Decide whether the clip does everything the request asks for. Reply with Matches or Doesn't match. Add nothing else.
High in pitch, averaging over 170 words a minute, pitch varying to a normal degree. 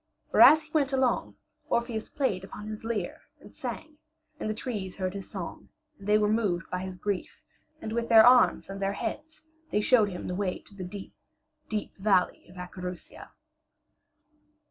Matches